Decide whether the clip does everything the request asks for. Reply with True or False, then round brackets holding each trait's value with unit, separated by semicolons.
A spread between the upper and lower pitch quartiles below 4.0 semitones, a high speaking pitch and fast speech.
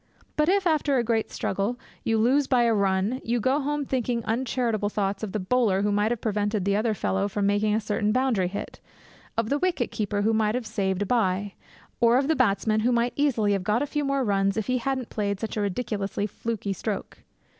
True (3.6 semitones; 220 Hz; 220 wpm)